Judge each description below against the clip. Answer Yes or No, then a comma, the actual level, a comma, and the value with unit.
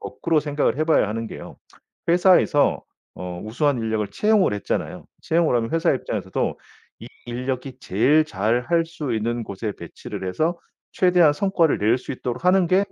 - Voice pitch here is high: No, medium, 140 Hz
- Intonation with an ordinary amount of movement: No, wide, 6.6 semitones